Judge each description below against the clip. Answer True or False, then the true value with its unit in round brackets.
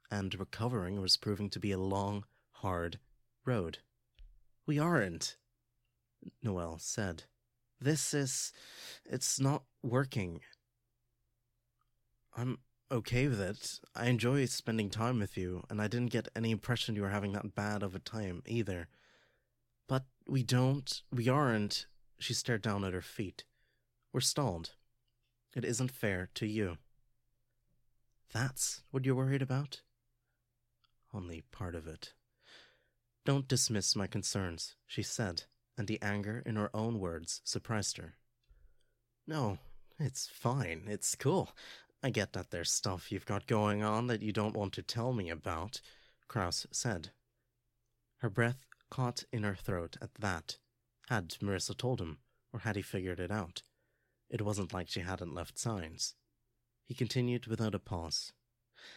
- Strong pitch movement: False (3.3 semitones)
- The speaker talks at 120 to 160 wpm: True (140 wpm)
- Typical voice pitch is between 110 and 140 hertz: True (115 Hz)